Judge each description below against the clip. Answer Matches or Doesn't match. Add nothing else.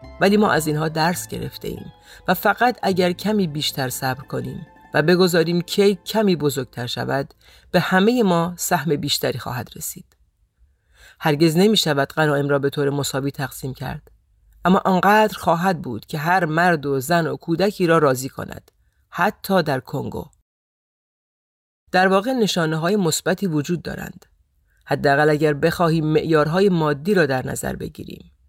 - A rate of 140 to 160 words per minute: Matches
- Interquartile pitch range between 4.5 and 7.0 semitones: Matches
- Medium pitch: Matches